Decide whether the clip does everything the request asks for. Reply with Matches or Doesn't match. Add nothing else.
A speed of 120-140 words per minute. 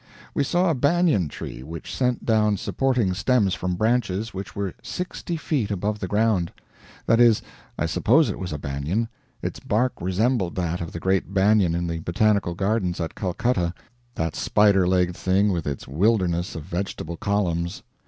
Doesn't match